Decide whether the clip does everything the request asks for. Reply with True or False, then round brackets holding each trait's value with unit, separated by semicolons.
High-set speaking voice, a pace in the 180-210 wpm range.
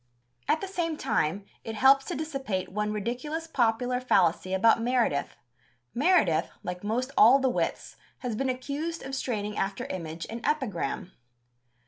False (240 Hz; 145 wpm)